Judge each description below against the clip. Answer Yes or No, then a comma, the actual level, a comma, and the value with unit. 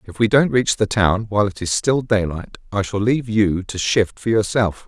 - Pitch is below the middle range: Yes, low, 105 Hz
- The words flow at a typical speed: No, fast, 235 wpm